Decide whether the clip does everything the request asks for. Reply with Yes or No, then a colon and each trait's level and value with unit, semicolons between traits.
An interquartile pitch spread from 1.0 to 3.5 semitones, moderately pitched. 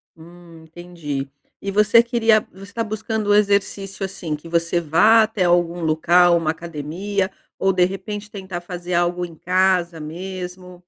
Yes: average, 2.9 semitones; medium, 180 Hz